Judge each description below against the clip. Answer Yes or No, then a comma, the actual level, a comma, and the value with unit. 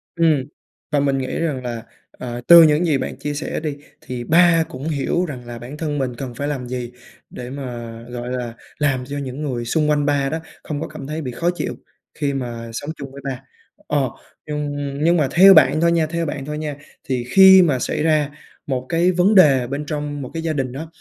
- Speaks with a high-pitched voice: No, medium, 145 Hz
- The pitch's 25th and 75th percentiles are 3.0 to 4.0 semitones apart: Yes, average, 3.5 semitones